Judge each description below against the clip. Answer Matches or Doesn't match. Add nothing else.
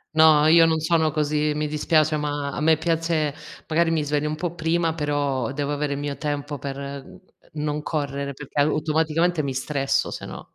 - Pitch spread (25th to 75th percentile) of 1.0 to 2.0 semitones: Matches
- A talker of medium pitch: Matches